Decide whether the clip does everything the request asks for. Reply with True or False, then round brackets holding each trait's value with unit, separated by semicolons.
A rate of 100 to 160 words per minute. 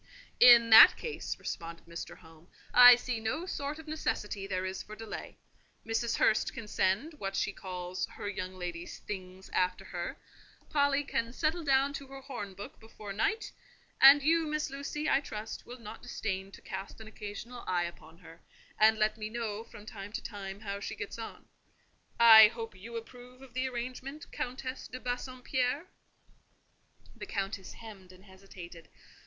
False (170 wpm)